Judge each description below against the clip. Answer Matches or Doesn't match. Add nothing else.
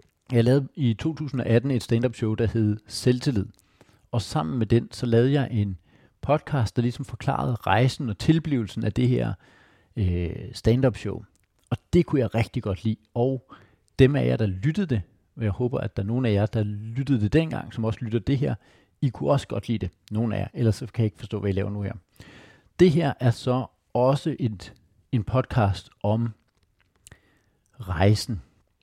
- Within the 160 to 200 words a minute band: Matches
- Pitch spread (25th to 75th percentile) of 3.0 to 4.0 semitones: Matches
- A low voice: Matches